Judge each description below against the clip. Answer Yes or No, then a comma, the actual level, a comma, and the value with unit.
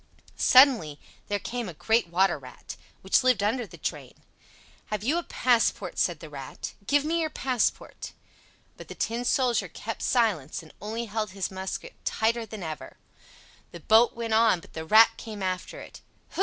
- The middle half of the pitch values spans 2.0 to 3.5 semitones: No, average, 4.5 semitones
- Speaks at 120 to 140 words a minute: No, average, 175 wpm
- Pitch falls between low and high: No, high, 220 Hz